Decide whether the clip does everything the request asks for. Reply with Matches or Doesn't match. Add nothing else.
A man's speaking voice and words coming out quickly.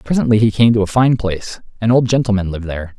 Matches